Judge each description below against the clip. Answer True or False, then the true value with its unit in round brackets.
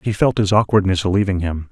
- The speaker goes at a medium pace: False (210 wpm)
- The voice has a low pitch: True (95 Hz)